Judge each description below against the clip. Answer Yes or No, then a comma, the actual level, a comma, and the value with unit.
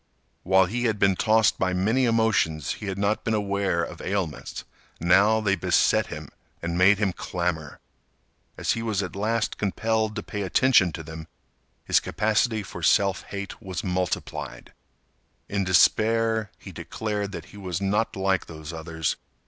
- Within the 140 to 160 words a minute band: Yes, average, 155 wpm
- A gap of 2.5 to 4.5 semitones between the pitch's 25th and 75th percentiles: Yes, average, 3.3 semitones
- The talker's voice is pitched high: No, low, 100 Hz